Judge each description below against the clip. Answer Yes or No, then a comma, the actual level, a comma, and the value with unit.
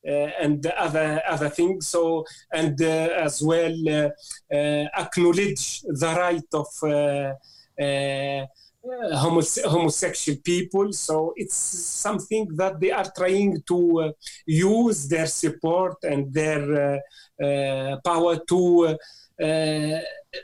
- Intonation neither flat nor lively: Yes, average, 3.1 semitones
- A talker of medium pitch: Yes, medium, 160 Hz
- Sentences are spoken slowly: Yes, slow, 120 wpm